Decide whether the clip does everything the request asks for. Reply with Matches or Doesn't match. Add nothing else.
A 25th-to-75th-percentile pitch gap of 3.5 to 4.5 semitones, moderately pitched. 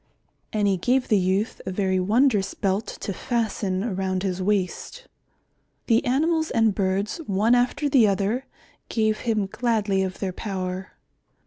Doesn't match